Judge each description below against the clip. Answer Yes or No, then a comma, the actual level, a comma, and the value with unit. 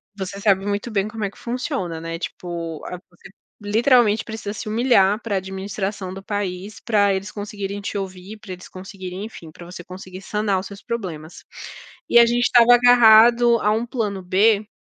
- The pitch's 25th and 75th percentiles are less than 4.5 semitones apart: Yes, average, 2.9 semitones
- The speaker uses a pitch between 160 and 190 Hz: No, high, 205 Hz